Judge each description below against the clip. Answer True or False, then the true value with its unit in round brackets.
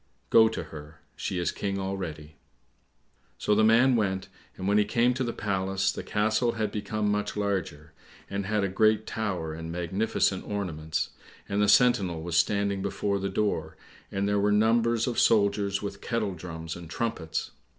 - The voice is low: True (100 Hz)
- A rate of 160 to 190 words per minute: True (170 wpm)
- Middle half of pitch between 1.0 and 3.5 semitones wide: True (3.2 semitones)